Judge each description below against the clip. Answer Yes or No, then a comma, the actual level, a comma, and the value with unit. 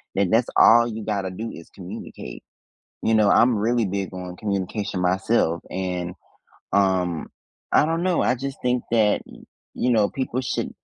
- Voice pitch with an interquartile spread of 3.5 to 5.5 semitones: Yes, average, 4.2 semitones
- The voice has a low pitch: Yes, low, 105 Hz